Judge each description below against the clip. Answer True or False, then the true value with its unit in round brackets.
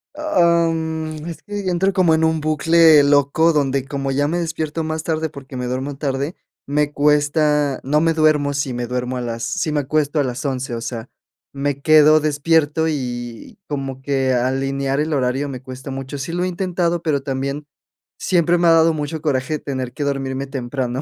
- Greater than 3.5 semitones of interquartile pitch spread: False (3.1 semitones)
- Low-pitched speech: False (145 Hz)